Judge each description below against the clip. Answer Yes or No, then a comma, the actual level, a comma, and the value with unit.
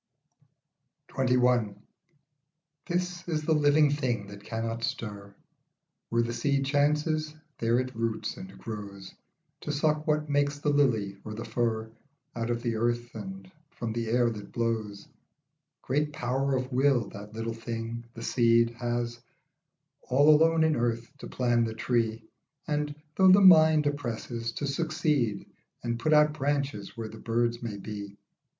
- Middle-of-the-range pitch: No, low, 120 Hz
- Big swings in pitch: No, average, 4.4 semitones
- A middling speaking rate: Yes, average, 150 wpm